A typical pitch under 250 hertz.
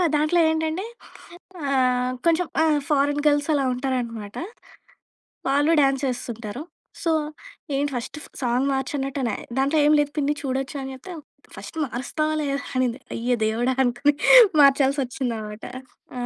No: very high, 270 Hz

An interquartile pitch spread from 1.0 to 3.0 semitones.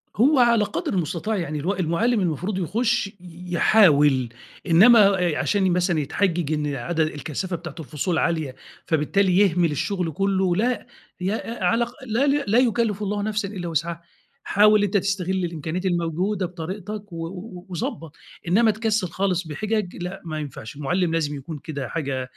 No: average, 4.3 semitones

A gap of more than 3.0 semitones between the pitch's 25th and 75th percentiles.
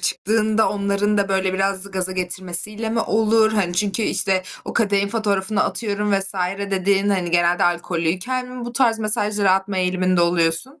No: narrow, 2.5 semitones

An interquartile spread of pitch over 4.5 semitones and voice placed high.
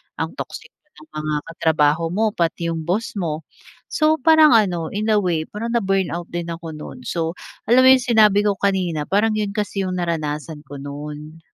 No: average, 5.0 semitones; medium, 180 Hz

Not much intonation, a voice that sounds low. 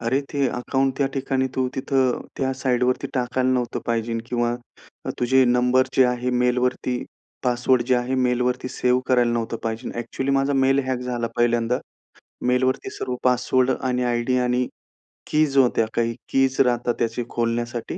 Yes: narrow, 1.4 semitones; low, 125 Hz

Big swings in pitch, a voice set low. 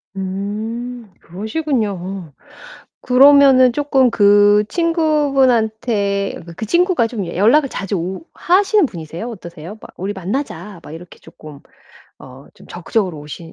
No: wide, 6.2 semitones; high, 210 Hz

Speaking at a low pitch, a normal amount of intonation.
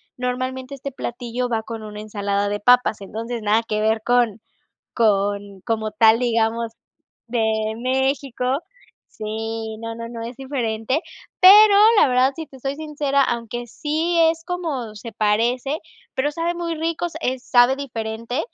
No: high, 240 Hz; average, 3.6 semitones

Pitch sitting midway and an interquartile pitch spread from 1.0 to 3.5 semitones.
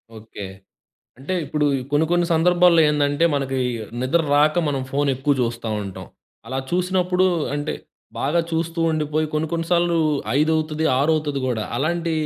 Yes: medium, 155 Hz; average, 3.0 semitones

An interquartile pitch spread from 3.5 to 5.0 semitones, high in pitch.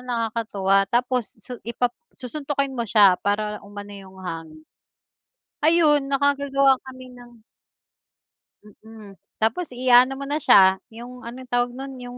Yes: average, 4.2 semitones; high, 245 Hz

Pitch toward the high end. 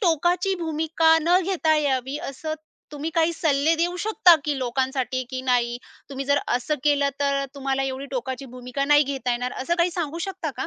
Yes: very high, 285 Hz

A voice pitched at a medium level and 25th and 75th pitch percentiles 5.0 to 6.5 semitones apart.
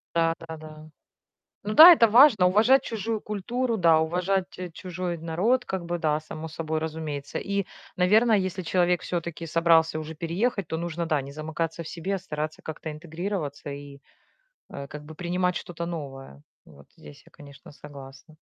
No: medium, 165 Hz; average, 3.3 semitones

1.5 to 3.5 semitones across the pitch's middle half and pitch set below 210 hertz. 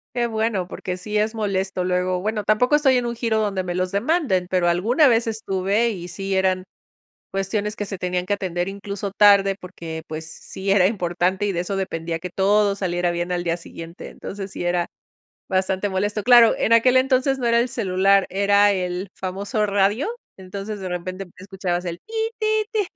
Yes: average, 2.8 semitones; high, 195 Hz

